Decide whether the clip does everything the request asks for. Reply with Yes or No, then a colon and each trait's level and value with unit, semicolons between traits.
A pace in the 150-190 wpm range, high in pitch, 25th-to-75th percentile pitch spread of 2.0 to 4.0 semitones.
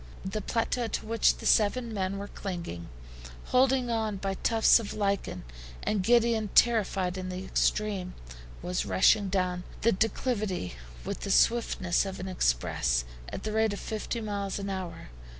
Yes: average, 160 wpm; high, 200 Hz; average, 3.2 semitones